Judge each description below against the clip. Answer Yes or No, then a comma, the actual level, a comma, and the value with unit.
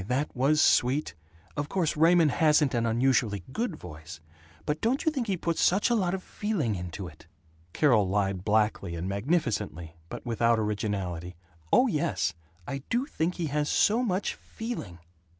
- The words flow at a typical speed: Yes, average, 165 wpm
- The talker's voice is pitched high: No, low, 130 Hz